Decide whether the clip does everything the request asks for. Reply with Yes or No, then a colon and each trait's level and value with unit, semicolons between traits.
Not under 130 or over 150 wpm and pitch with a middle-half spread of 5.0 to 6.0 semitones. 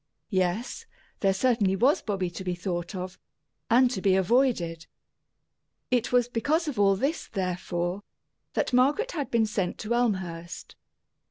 Yes: average, 145 wpm; average, 5.3 semitones